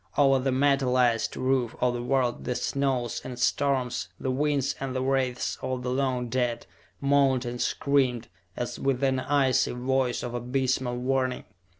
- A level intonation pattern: Yes, narrow, 1.7 semitones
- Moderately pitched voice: No, low, 130 Hz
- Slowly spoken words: No, average, 160 wpm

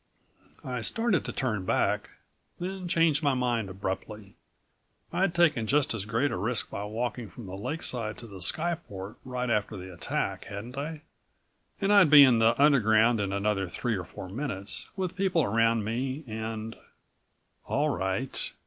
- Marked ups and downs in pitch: Yes, wide, 5.9 semitones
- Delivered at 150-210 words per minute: Yes, average, 160 wpm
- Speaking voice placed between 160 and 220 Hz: No, low, 115 Hz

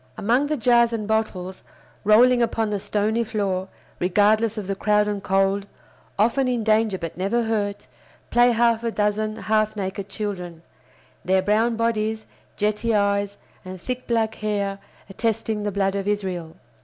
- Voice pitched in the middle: No, high, 210 Hz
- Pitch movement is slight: Yes, narrow, 2.2 semitones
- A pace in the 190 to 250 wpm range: No, average, 155 wpm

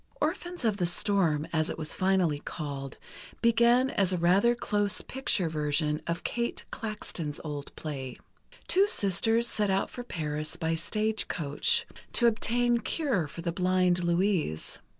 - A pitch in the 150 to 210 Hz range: Yes, medium, 185 Hz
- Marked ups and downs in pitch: Yes, wide, 6.7 semitones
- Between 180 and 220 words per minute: No, average, 150 wpm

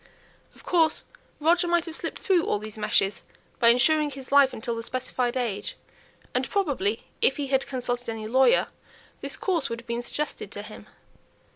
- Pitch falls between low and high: No, very high, 260 Hz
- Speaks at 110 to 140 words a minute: No, average, 175 wpm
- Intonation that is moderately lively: Yes, average, 5.0 semitones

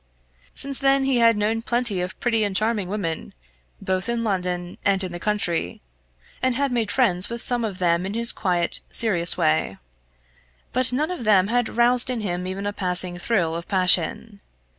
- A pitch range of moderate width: Yes, average, 4.7 semitones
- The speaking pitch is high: Yes, high, 205 Hz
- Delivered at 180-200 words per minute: Yes, average, 185 wpm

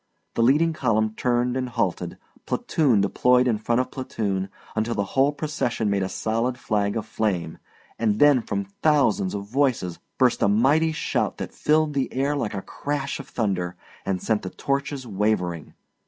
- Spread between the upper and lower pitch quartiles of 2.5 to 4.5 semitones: No, average, 5.2 semitones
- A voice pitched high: No, low, 115 Hz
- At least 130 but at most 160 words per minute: No, average, 170 wpm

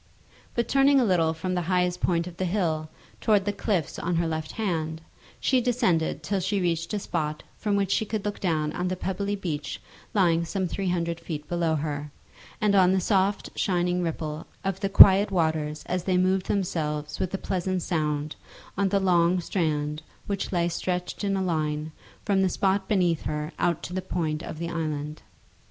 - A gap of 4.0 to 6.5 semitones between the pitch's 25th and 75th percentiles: No, average, 3.3 semitones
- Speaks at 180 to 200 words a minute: Yes, average, 190 wpm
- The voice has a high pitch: No, medium, 180 Hz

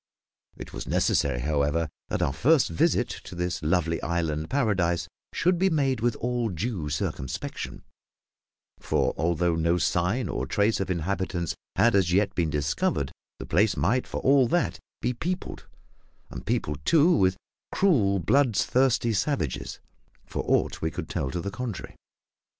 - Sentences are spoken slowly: No, average, 150 wpm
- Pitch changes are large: Yes, wide, 7.0 semitones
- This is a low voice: Yes, very low, 95 Hz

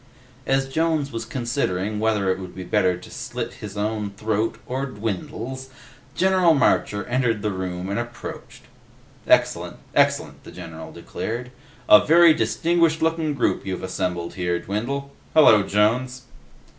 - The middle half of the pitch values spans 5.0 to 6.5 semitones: Yes, wide, 5.5 semitones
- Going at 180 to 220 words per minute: No, average, 140 wpm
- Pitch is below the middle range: Yes, low, 110 Hz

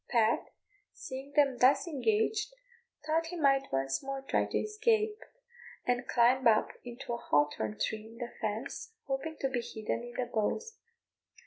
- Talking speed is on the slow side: No, average, 155 wpm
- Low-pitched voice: No, very high, 255 Hz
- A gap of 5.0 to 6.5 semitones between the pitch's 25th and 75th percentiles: Yes, average, 5.3 semitones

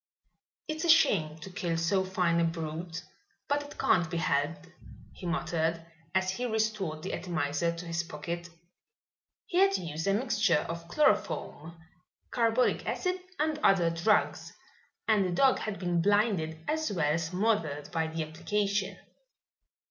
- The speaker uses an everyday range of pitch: Yes, average, 4.5 semitones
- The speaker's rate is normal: Yes, average, 150 wpm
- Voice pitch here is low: No, medium, 175 Hz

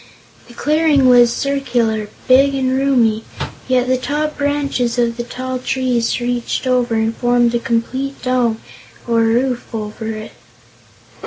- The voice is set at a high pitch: Yes, high, 245 Hz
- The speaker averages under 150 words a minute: Yes, average, 140 wpm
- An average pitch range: No, narrow, 2.2 semitones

